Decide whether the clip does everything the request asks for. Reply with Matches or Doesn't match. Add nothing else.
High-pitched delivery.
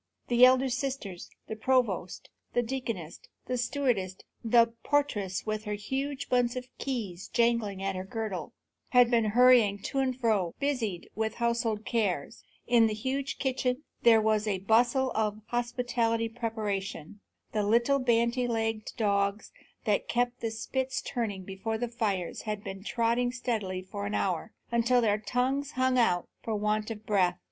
Matches